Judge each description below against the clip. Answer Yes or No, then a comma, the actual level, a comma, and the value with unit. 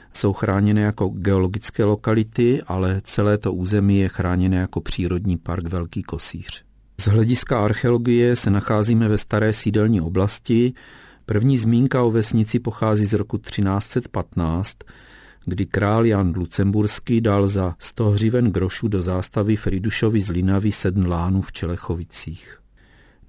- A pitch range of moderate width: Yes, average, 3.1 semitones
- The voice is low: Yes, low, 105 Hz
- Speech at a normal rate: Yes, average, 130 wpm